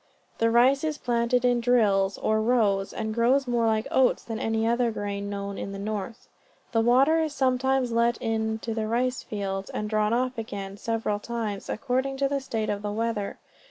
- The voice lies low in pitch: No, high, 230 Hz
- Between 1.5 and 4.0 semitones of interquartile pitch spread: Yes, average, 2.8 semitones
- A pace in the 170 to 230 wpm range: Yes, average, 200 wpm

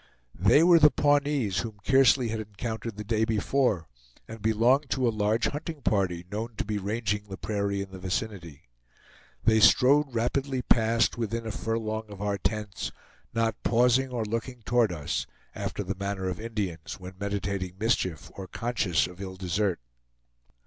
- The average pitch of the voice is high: No, low, 110 Hz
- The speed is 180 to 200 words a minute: No, average, 165 wpm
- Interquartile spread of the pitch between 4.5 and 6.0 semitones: No, average, 3.1 semitones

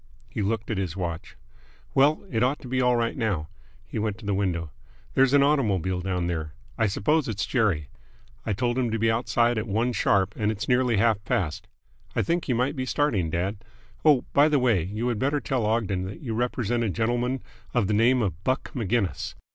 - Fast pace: Yes, fast, 210 wpm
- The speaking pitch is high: No, low, 115 Hz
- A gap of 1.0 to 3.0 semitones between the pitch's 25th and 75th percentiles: No, average, 4.2 semitones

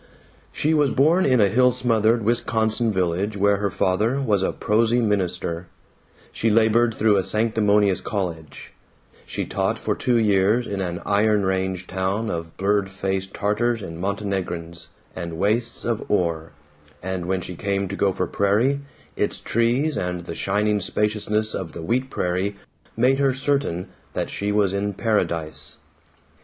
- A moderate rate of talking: Yes, average, 150 wpm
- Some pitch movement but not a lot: Yes, average, 3.3 semitones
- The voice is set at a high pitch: No, low, 100 Hz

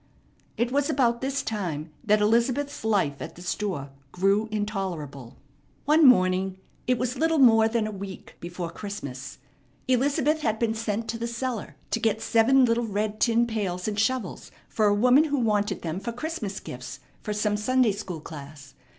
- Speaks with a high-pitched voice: Yes, high, 215 Hz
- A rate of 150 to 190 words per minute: Yes, average, 170 wpm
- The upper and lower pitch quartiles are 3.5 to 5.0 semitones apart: Yes, average, 4.1 semitones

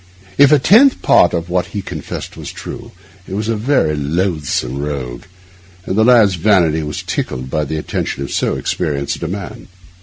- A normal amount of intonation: No, wide, 5.9 semitones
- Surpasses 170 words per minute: Yes, average, 180 wpm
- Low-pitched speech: Yes, very low, 85 Hz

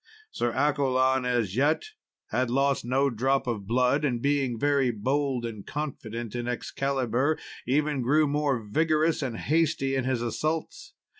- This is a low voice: Yes, low, 130 Hz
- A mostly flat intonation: No, average, 3.1 semitones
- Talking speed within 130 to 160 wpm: Yes, average, 145 wpm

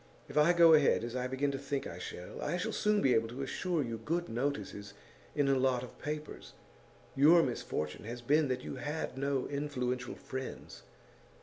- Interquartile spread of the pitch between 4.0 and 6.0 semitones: No, average, 3.3 semitones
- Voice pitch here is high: No, low, 135 Hz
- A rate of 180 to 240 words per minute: Yes, average, 190 wpm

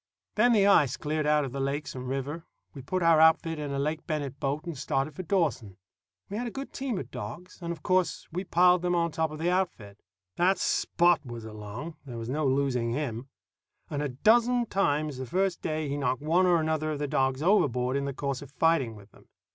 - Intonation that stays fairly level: No, average, 4.5 semitones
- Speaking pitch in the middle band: Yes, medium, 150 Hz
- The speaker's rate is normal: No, fast, 220 wpm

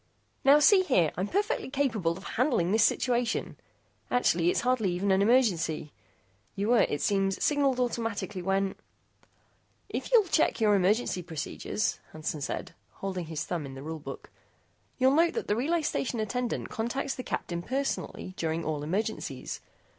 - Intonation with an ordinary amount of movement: No, wide, 6.7 semitones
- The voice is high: Yes, high, 210 Hz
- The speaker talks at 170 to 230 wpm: No, average, 160 wpm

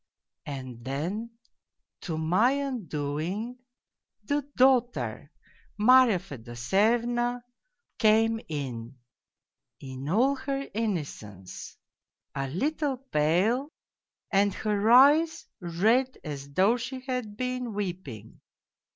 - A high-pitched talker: Yes, high, 210 Hz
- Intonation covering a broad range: Yes, wide, 9.0 semitones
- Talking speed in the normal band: No, slow, 90 wpm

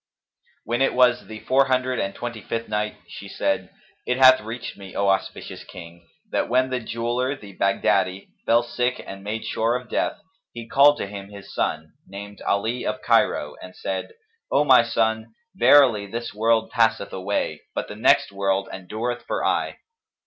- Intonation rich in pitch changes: No, average, 3.8 semitones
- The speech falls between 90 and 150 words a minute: No, average, 175 wpm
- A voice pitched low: Yes, low, 115 Hz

